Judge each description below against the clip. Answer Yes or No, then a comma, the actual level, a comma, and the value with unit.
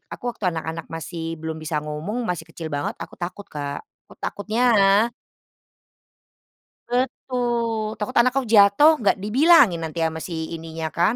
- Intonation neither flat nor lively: No, wide, 6.7 semitones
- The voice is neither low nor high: No, high, 195 Hz